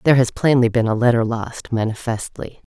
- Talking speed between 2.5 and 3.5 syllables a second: No, 5.5 syllables/s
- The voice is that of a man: No, female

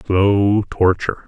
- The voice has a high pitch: No, low, 100 Hz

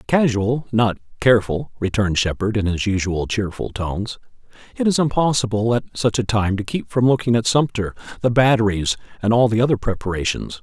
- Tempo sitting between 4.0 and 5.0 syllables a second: No, 5.6 syllables/s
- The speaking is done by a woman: No, male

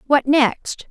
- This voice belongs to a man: No, female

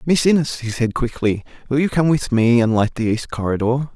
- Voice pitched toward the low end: Yes, low, 125 Hz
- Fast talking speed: Yes, fast, 225 wpm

